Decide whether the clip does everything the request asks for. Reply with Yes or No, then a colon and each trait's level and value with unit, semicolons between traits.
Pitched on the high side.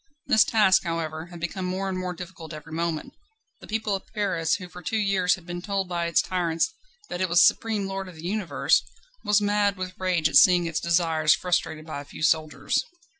No: medium, 180 Hz